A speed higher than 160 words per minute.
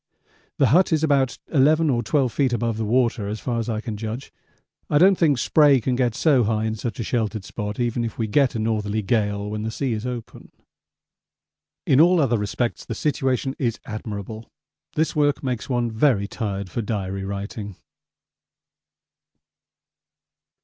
Yes: average, 170 wpm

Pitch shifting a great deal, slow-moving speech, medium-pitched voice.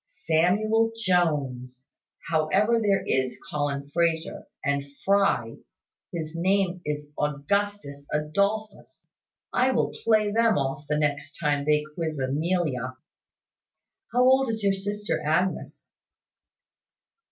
Yes: wide, 5.9 semitones; slow, 105 wpm; medium, 165 Hz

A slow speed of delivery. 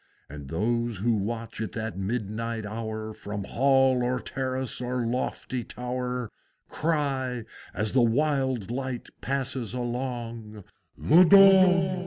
Yes: slow, 120 wpm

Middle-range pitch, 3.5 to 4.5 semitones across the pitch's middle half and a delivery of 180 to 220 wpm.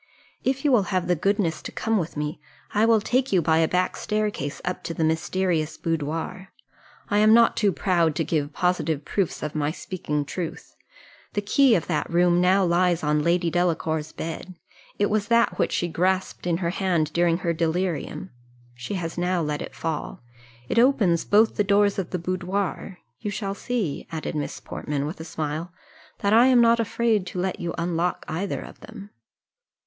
Yes: medium, 180 Hz; average, 3.9 semitones; average, 190 wpm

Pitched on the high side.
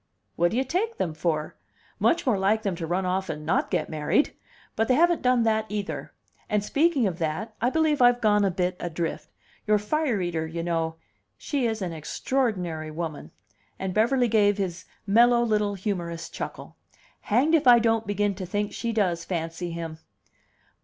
Yes: high, 205 Hz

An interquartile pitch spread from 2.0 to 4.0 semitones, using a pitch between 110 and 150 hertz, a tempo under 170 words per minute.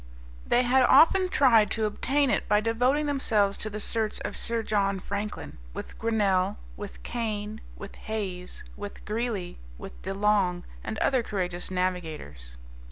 No: average, 3.2 semitones; high, 210 Hz; average, 150 wpm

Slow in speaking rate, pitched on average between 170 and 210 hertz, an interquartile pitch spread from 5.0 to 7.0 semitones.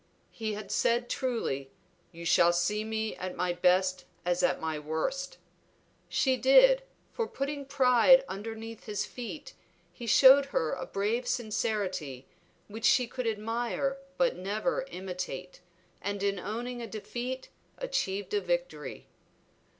No: slow, 130 wpm; high, 220 Hz; wide, 5.6 semitones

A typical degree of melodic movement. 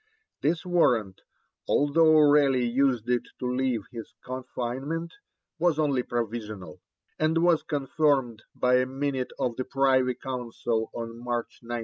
Yes: average, 3.4 semitones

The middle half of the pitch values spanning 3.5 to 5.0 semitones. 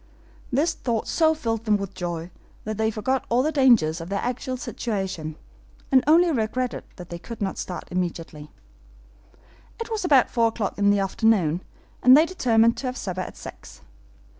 No: wide, 5.6 semitones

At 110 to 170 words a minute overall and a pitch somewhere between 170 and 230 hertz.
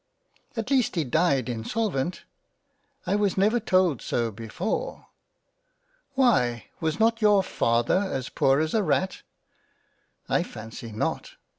Yes: average, 155 wpm; medium, 185 Hz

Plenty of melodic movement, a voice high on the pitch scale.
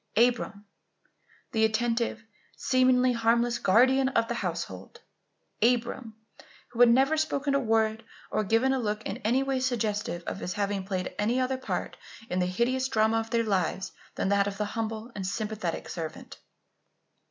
No: average, 3.4 semitones; high, 225 Hz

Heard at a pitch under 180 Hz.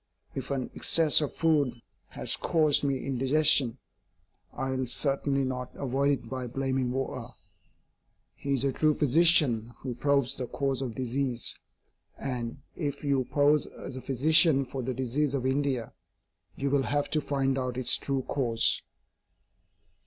Yes: low, 135 Hz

